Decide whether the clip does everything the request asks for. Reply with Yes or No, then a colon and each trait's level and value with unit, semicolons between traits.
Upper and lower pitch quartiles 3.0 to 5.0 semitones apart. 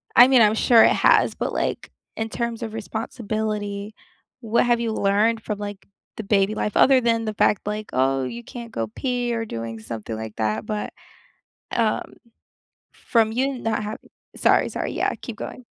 No: narrow, 2.6 semitones